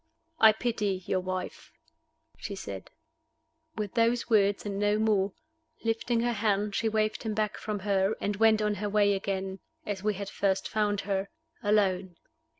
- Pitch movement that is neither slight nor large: No, narrow, 1.8 semitones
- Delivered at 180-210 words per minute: No, average, 160 wpm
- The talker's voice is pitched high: Yes, high, 205 Hz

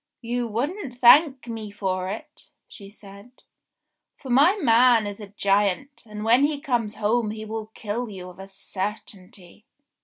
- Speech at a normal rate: Yes, average, 155 wpm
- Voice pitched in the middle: No, high, 220 Hz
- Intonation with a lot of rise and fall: No, average, 3.5 semitones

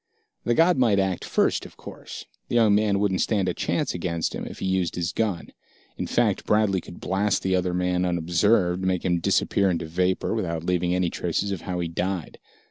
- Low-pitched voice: Yes, very low, 90 Hz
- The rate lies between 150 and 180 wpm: No, fast, 205 wpm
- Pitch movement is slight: Yes, narrow, 2.3 semitones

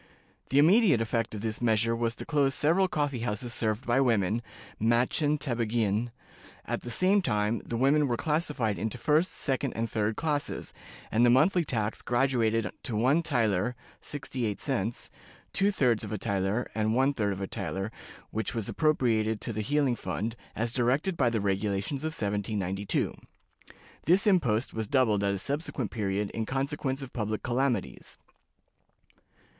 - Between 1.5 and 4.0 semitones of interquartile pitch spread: No, average, 4.5 semitones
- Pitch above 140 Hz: No, low, 120 Hz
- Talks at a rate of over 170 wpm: No, average, 160 wpm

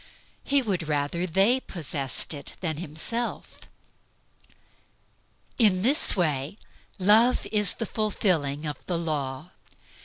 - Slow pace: Yes, slow, 110 wpm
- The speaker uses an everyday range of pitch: No, wide, 6.1 semitones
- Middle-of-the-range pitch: Yes, medium, 175 Hz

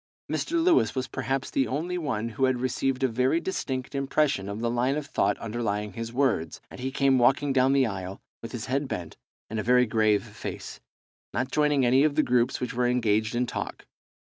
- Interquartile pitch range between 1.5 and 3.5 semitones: Yes, average, 2.9 semitones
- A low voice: Yes, low, 125 Hz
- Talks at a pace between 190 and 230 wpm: Yes, fast, 205 wpm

